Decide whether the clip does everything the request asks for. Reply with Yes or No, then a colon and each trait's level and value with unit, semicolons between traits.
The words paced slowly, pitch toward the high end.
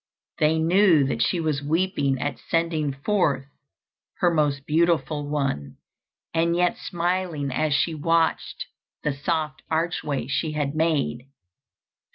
No: slow, 125 wpm; medium, 155 Hz